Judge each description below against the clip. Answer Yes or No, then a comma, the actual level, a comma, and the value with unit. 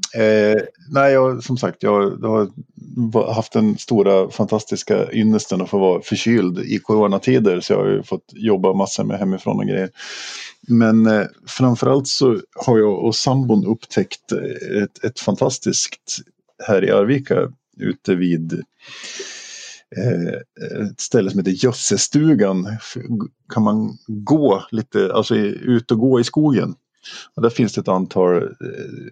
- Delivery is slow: No, average, 140 wpm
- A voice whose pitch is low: Yes, low, 110 Hz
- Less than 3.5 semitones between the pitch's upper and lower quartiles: No, average, 3.9 semitones